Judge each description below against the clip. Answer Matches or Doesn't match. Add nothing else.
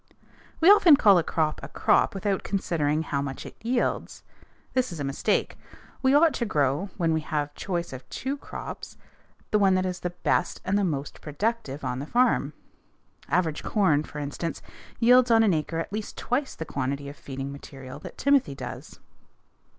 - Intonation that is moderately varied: Doesn't match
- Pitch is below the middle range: Doesn't match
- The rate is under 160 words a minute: Doesn't match